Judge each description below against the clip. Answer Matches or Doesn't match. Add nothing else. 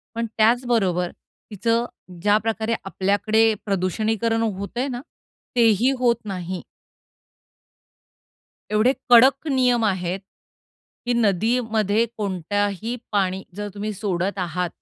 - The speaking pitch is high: Matches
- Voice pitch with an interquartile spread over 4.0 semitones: Doesn't match